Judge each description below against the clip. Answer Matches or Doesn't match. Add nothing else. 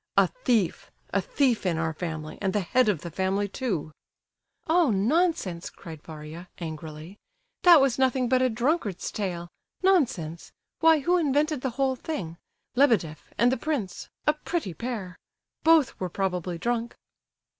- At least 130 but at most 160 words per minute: Matches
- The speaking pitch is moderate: Doesn't match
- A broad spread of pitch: Matches